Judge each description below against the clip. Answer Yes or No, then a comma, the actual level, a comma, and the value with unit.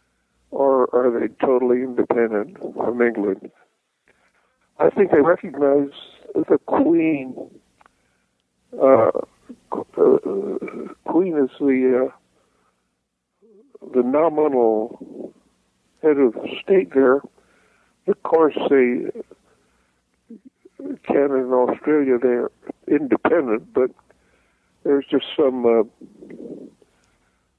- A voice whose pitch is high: No, medium, 140 Hz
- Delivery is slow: Yes, slow, 80 wpm